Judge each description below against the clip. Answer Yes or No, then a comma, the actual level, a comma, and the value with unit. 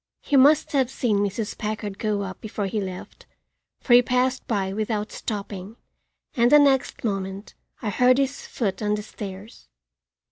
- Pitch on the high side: Yes, high, 215 Hz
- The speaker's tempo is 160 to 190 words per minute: Yes, average, 165 wpm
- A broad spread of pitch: No, average, 3.7 semitones